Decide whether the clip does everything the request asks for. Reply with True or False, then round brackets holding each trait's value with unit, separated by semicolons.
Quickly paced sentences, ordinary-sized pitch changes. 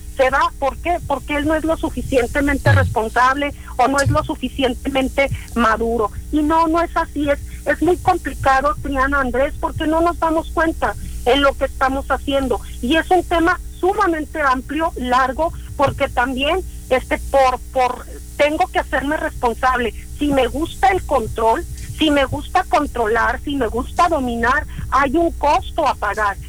False (165 wpm; 4.0 semitones)